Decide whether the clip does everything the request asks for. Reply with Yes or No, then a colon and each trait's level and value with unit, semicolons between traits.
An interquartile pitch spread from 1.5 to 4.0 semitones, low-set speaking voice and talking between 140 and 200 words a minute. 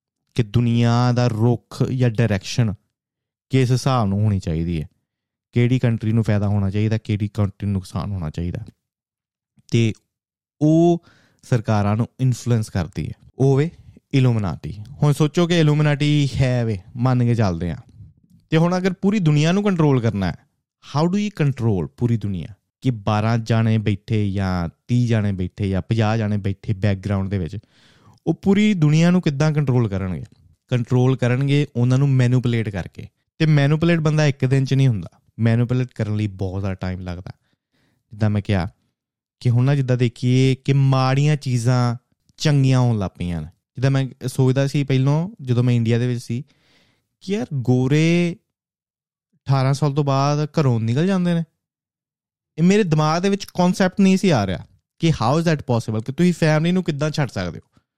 No: wide, 5.5 semitones; low, 125 Hz; fast, 165 wpm